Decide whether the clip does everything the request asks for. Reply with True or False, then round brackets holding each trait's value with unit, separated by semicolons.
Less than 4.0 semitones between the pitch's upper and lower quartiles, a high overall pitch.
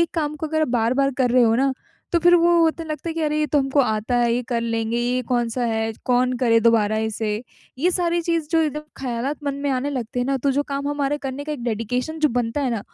False (4.3 semitones; 265 Hz)